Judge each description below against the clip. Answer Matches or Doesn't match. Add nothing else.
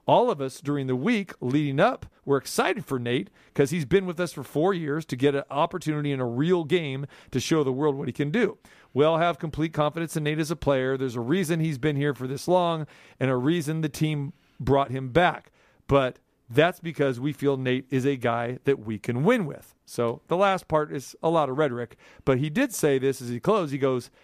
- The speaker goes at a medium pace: Doesn't match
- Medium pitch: Matches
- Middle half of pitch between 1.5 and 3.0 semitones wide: Doesn't match